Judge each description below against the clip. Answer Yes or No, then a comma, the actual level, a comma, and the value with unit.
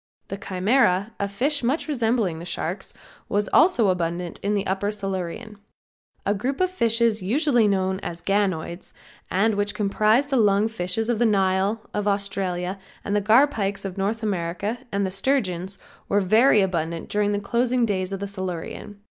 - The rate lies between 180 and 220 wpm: No, average, 165 wpm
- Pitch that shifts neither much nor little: Yes, average, 3.0 semitones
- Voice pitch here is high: Yes, high, 200 Hz